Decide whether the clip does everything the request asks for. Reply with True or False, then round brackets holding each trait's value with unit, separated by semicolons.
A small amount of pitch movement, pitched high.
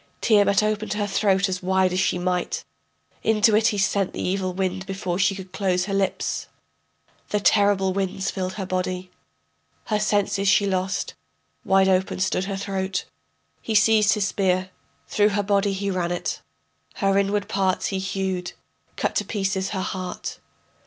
True (1.5 semitones; 195 Hz)